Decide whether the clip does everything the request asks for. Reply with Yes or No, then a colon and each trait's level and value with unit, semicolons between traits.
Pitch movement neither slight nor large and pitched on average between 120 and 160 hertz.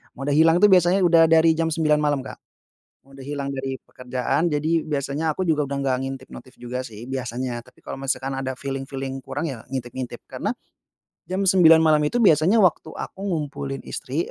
Yes: average, 3.4 semitones; medium, 140 Hz